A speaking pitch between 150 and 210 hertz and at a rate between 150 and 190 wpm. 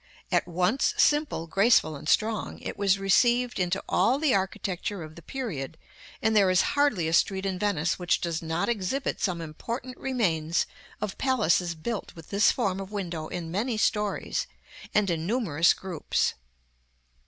Yes: high, 190 Hz; average, 160 wpm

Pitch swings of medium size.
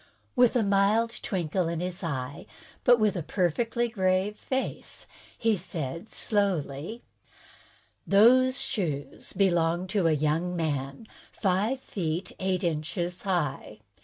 Yes: average, 4.6 semitones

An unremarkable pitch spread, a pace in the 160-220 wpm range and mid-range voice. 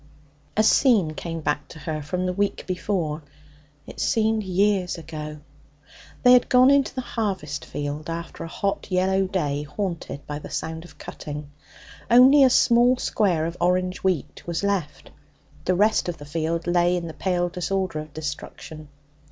Yes: average, 4.4 semitones; average, 165 wpm; medium, 175 Hz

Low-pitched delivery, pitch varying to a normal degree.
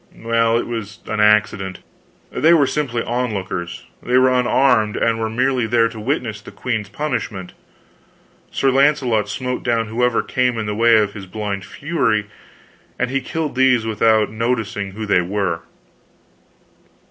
Yes: low, 115 Hz; average, 3.1 semitones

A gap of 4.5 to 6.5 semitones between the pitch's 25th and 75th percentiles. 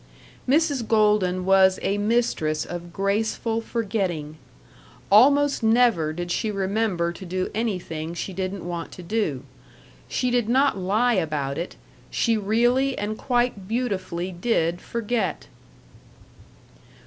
Yes: average, 4.8 semitones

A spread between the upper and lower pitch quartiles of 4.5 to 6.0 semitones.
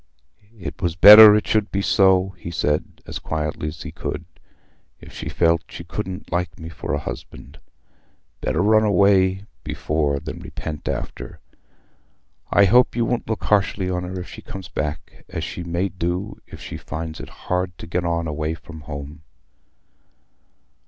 No: average, 3.5 semitones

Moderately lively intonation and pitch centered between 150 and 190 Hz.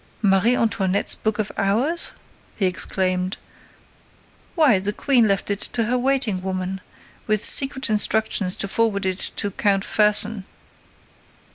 No: average, 3.0 semitones; high, 205 Hz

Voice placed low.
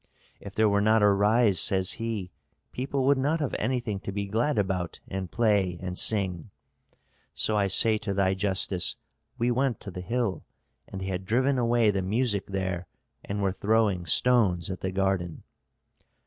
Yes: low, 100 Hz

